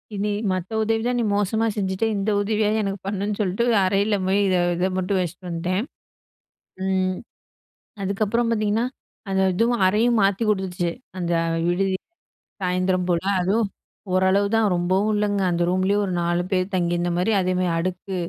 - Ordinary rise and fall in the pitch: No, narrow, 2.3 semitones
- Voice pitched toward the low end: No, high, 190 Hz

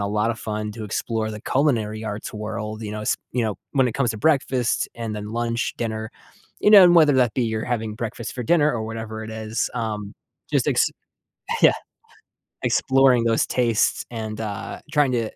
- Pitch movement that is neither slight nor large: No, narrow, 2.3 semitones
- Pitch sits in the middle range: No, low, 115 Hz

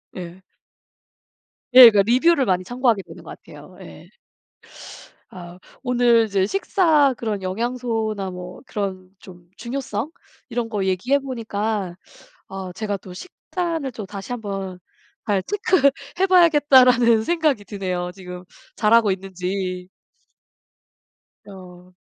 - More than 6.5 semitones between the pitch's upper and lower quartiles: No, average, 5.2 semitones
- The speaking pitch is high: Yes, high, 215 Hz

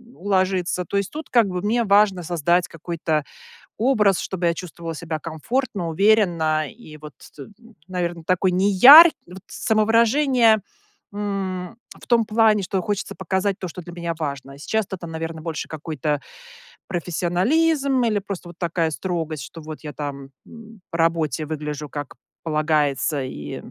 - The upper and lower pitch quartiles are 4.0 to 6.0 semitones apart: Yes, average, 4.6 semitones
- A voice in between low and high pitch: Yes, medium, 180 Hz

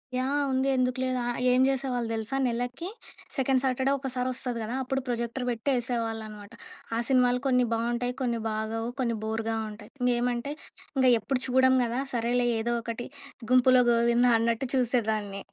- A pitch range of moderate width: No, narrow, 1.9 semitones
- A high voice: Yes, high, 245 Hz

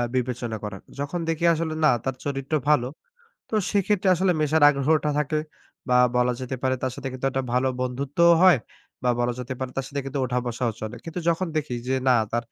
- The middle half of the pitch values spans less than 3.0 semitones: No, average, 3.7 semitones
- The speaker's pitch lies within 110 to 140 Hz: Yes, low, 135 Hz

